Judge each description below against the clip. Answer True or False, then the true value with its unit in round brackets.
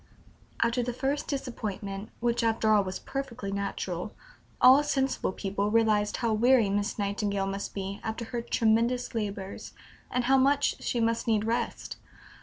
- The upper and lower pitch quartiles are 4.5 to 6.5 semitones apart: False (3.4 semitones)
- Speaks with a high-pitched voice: True (225 Hz)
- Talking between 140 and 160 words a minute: True (155 wpm)